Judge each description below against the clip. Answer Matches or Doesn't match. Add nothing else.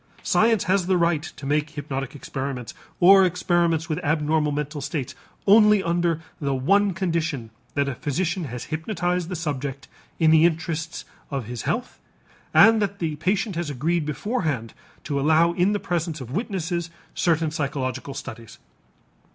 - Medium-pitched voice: Matches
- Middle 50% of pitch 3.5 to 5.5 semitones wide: Matches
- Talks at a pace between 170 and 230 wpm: Doesn't match